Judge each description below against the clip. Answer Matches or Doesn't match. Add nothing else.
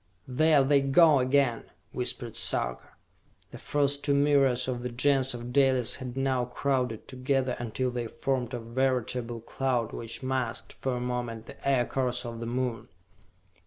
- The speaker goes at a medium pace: Matches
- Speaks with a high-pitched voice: Doesn't match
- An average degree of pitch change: Doesn't match